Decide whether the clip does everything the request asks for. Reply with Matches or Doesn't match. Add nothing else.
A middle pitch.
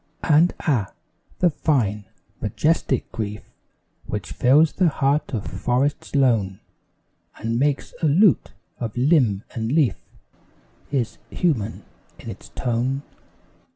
Doesn't match